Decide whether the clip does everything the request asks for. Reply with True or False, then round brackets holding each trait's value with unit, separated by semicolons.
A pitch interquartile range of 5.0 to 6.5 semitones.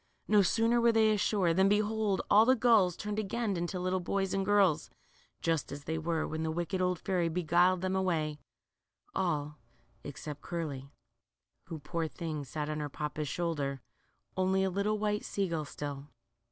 False (4.3 semitones)